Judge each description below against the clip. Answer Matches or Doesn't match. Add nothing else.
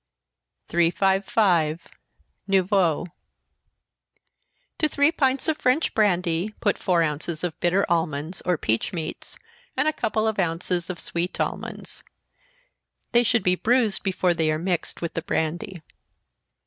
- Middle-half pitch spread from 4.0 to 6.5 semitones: Matches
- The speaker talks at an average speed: Doesn't match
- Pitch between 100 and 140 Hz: Doesn't match